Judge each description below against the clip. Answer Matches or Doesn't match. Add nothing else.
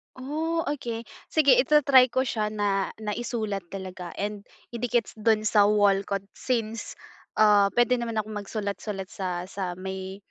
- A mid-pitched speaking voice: Doesn't match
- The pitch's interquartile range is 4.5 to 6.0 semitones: Doesn't match